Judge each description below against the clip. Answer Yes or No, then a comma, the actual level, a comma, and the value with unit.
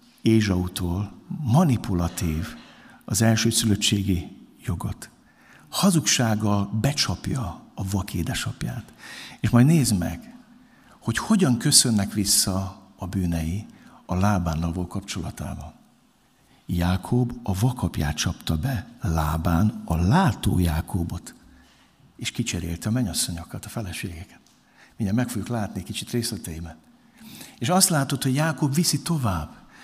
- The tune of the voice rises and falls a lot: Yes, wide, 5.8 semitones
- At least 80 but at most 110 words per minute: Yes, slow, 105 wpm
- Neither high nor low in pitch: No, low, 105 Hz